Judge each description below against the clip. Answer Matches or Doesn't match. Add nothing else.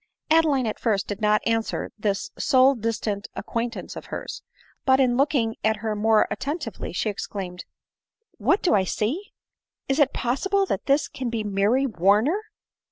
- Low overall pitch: Doesn't match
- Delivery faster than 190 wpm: Doesn't match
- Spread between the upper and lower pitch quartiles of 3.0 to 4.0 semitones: Doesn't match